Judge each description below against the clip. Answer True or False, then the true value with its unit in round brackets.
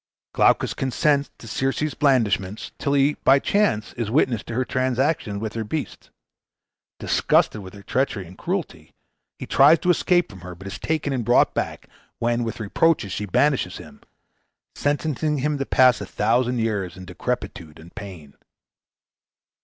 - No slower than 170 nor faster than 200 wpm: False (160 wpm)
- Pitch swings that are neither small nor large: False (5.9 semitones)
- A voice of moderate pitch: False (120 Hz)